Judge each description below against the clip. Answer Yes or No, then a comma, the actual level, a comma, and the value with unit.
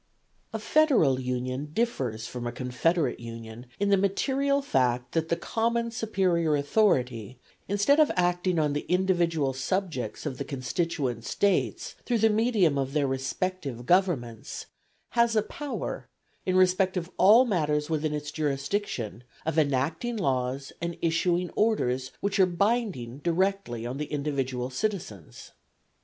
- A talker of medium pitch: Yes, medium, 160 Hz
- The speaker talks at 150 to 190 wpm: No, average, 140 wpm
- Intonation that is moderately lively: No, wide, 7.1 semitones